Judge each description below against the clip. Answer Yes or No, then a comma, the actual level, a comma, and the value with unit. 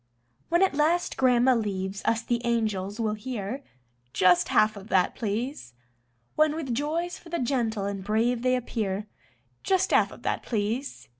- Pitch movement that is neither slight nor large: Yes, average, 4.8 semitones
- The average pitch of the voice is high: Yes, high, 235 Hz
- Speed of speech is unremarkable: Yes, average, 160 wpm